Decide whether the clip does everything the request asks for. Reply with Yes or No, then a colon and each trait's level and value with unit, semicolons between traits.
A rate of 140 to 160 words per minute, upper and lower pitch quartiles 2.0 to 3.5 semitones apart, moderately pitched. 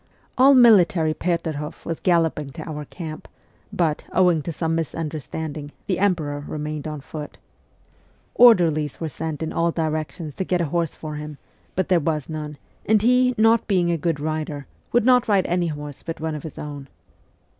No: average, 180 wpm; average, 2.9 semitones; medium, 160 Hz